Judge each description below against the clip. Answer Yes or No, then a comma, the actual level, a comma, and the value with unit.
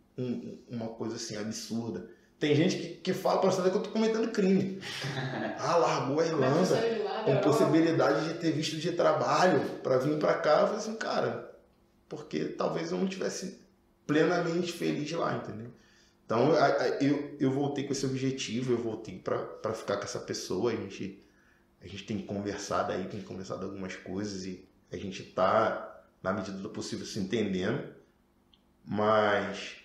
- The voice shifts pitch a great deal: Yes, wide, 8.4 semitones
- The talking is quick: No, average, 160 wpm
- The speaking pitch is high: No, low, 135 Hz